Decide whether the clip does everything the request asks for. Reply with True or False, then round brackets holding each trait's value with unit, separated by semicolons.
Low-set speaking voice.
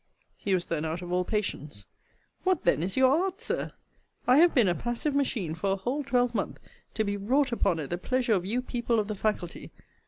False (215 Hz)